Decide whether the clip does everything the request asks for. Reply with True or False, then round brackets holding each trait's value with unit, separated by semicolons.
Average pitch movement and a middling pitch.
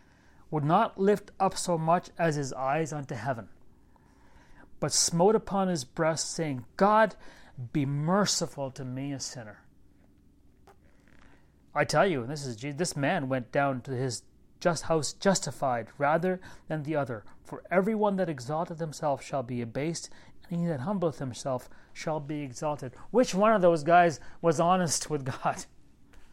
True (4.7 semitones; 150 Hz)